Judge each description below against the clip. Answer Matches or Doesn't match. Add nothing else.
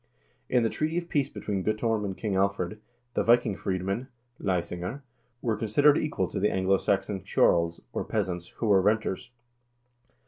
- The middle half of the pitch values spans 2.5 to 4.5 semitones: Matches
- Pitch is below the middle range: Matches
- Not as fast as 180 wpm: Matches